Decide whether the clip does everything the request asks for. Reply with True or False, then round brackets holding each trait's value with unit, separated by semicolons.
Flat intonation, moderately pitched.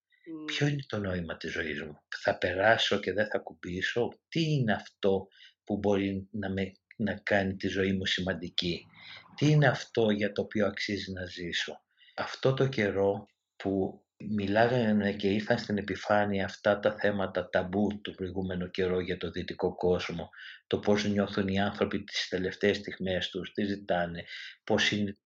False (1.9 semitones; 100 Hz)